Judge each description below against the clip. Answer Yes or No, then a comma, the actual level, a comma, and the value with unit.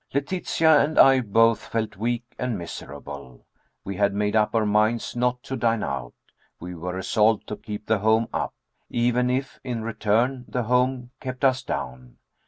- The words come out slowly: No, average, 170 wpm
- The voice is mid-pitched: No, low, 115 Hz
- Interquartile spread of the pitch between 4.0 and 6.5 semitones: No, average, 3.4 semitones